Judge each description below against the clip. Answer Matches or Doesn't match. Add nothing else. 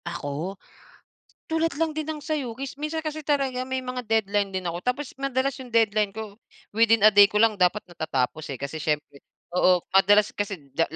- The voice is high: Matches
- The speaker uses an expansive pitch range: Matches